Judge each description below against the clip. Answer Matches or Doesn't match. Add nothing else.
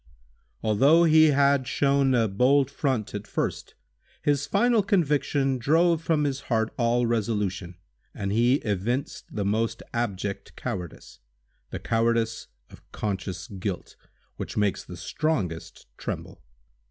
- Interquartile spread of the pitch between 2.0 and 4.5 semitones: Doesn't match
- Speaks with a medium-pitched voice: Doesn't match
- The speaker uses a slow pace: Matches